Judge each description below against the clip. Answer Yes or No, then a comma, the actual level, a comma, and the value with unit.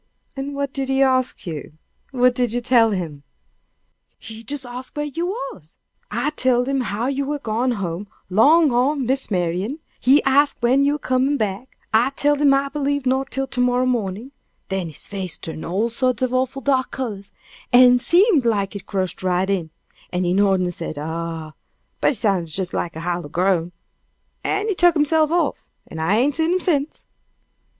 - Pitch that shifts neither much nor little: No, wide, 6.3 semitones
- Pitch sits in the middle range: No, high, 245 Hz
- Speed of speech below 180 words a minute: No, average, 190 wpm